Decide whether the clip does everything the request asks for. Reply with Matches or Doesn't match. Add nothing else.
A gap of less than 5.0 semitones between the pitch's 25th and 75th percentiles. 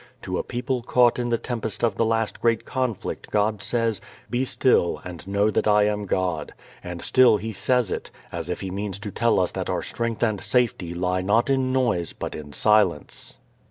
Matches